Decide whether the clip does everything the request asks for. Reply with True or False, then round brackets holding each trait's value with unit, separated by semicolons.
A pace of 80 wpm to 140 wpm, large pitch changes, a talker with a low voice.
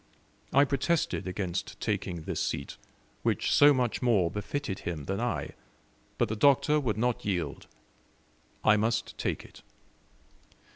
True (135 wpm; 6.3 semitones; 110 Hz)